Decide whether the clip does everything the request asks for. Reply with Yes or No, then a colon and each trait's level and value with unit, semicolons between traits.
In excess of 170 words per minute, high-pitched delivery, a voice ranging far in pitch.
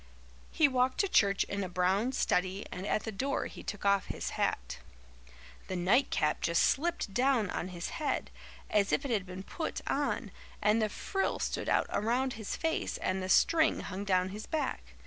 Yes: average, 185 wpm; high, 205 Hz; wide, 5.9 semitones